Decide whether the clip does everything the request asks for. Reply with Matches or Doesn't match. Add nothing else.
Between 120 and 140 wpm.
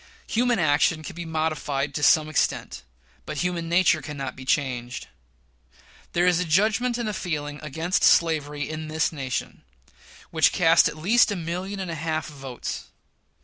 Doesn't match